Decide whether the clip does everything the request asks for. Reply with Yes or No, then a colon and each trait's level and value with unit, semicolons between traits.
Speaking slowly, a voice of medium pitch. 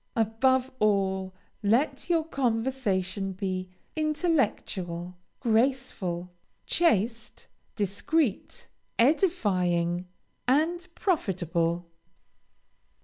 No: slow, 60 wpm; high, 220 Hz